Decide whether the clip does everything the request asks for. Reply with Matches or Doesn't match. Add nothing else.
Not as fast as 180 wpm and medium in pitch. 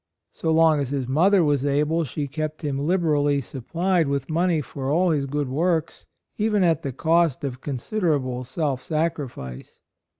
Matches